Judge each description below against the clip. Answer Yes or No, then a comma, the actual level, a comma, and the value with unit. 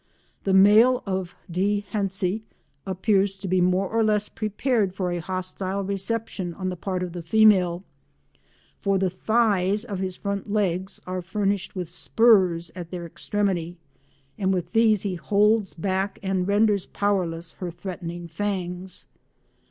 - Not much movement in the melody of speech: Yes, narrow, 2.2 semitones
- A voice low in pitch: No, high, 190 Hz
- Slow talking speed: No, average, 145 wpm